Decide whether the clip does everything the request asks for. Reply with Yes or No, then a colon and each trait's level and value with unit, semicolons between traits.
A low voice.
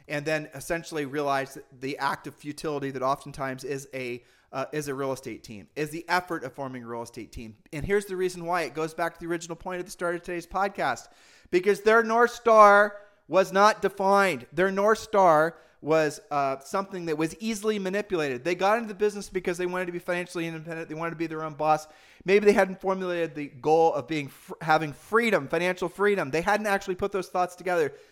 No: medium, 170 Hz